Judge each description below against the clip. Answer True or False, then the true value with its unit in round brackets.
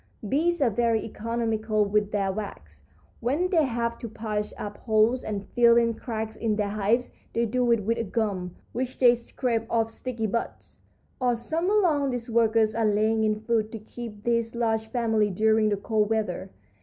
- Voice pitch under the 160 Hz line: False (225 Hz)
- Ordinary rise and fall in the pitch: False (1.9 semitones)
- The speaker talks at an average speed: True (180 wpm)